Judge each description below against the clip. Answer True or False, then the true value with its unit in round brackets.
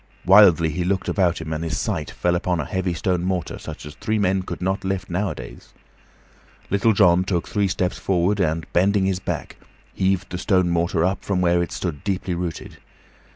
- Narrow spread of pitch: True (2.0 semitones)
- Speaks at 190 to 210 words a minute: True (195 wpm)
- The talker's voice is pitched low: True (90 Hz)